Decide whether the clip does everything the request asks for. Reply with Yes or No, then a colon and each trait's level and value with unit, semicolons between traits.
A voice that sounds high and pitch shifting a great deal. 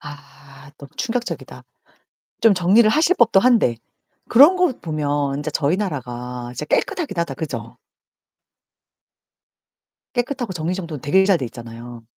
No: medium, 165 Hz; wide, 8.7 semitones